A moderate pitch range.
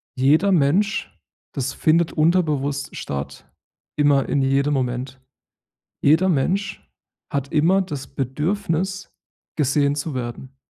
Yes: average, 4.0 semitones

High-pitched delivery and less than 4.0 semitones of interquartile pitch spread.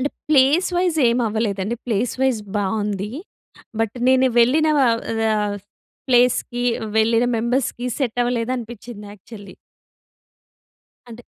Yes: high, 235 Hz; average, 3.1 semitones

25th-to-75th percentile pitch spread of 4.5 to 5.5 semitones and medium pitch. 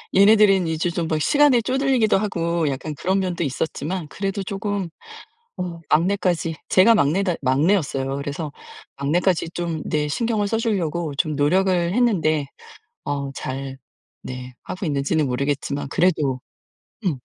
Yes: average, 5.2 semitones; medium, 170 Hz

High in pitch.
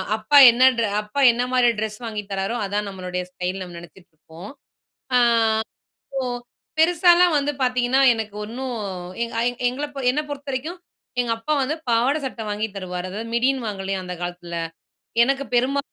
Yes: high, 230 Hz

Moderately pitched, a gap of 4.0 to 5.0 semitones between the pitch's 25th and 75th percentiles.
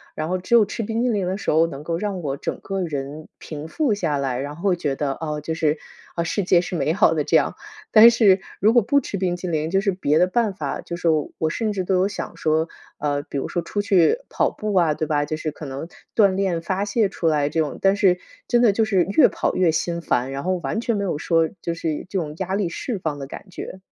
Yes: medium, 175 Hz; average, 4.3 semitones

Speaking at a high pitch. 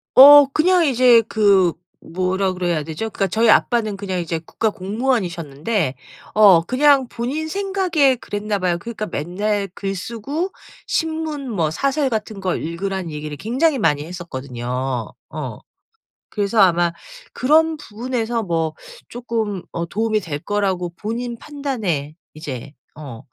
Yes: high, 205 Hz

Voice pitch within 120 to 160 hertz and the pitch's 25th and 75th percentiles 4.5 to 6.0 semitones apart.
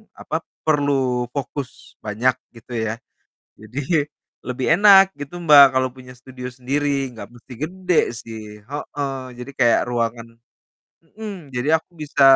No: low, 135 Hz; average, 3.6 semitones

